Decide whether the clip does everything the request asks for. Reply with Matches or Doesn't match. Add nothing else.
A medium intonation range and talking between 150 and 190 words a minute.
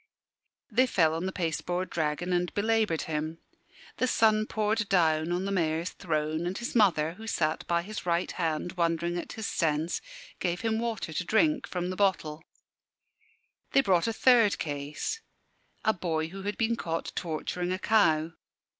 Matches